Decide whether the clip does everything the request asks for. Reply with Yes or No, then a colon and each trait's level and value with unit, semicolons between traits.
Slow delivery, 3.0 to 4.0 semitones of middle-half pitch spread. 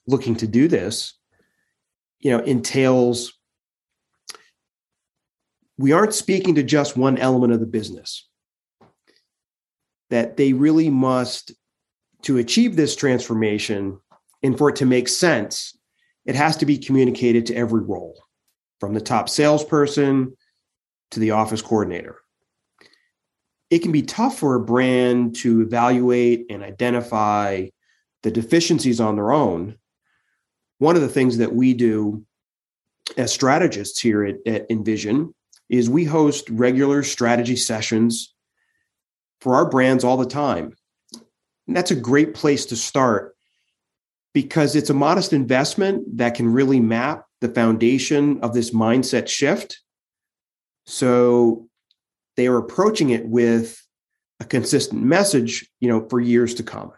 Yes: slow, 130 wpm; average, 3.7 semitones